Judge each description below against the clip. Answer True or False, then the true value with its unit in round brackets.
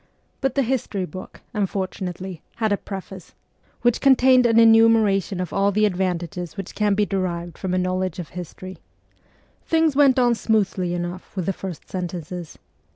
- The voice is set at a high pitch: True (195 Hz)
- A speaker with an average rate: True (155 wpm)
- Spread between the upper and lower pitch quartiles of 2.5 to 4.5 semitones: True (3.7 semitones)